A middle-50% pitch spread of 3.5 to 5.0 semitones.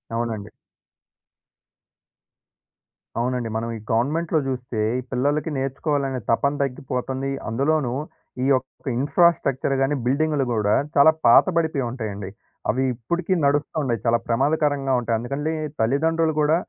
Yes: average, 3.8 semitones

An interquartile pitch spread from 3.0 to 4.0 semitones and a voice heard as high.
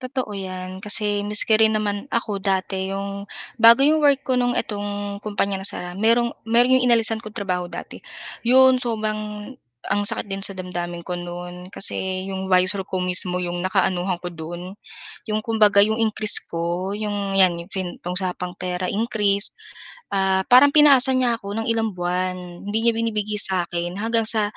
Yes: average, 3.3 semitones; high, 200 Hz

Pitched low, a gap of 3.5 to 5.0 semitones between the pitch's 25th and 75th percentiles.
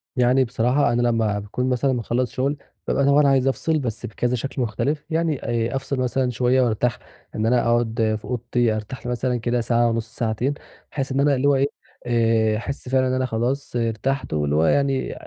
No: low, 125 Hz; average, 2.7 semitones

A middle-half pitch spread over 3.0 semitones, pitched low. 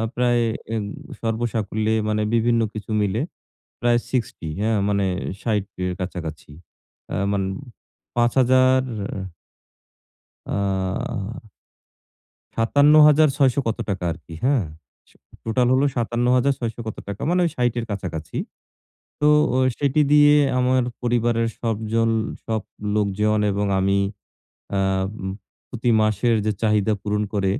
Yes: average, 3.5 semitones; low, 115 Hz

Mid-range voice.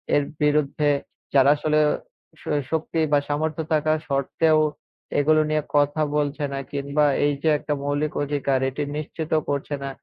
Yes: medium, 150 Hz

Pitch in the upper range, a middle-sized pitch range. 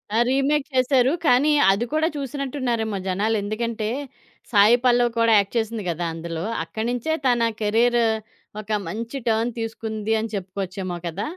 Yes: high, 225 Hz; average, 3.1 semitones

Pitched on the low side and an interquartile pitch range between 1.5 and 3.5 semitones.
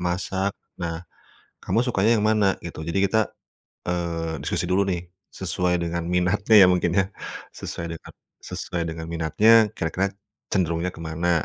Yes: very low, 90 Hz; average, 2.7 semitones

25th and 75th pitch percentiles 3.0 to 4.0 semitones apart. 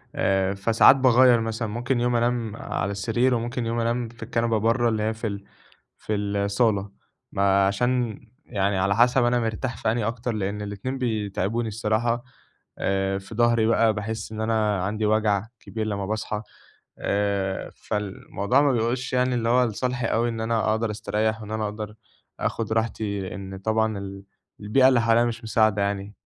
No: narrow, 2.5 semitones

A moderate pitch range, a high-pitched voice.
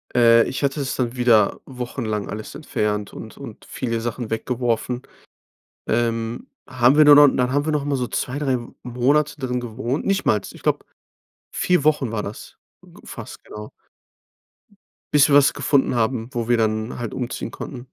No: average, 3.4 semitones; low, 125 Hz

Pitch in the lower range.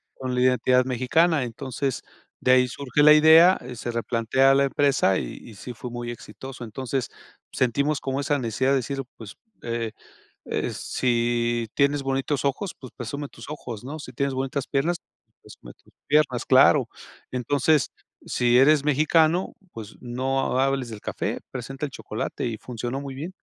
Yes: low, 130 Hz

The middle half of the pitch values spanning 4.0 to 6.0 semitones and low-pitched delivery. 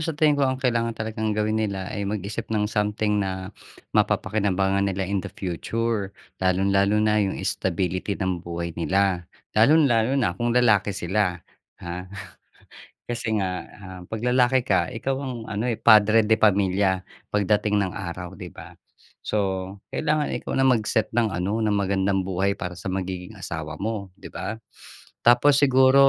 No: average, 3.2 semitones; low, 105 Hz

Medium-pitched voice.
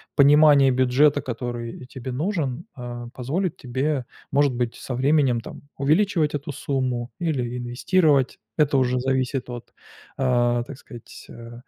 No: low, 130 Hz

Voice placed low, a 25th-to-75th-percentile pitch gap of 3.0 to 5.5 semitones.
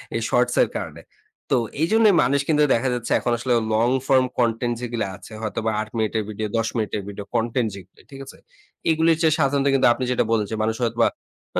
Yes: low, 120 Hz; average, 3.3 semitones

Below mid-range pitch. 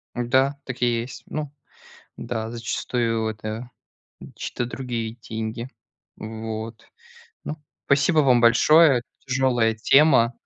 Yes: low, 120 Hz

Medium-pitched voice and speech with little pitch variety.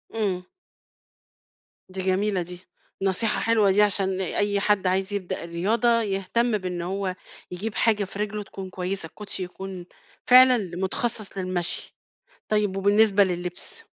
No: high, 195 Hz; narrow, 2.3 semitones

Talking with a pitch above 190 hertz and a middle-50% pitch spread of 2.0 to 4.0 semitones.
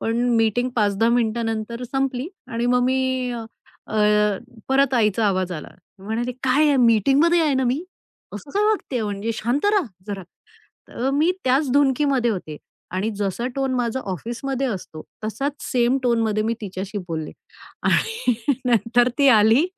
Yes: high, 240 Hz; average, 3.6 semitones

